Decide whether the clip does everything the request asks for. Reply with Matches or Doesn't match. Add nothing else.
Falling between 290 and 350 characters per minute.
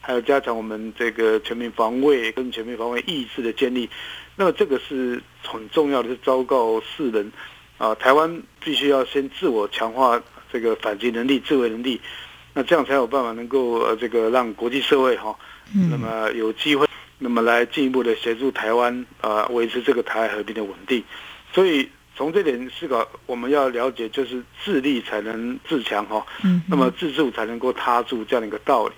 Matches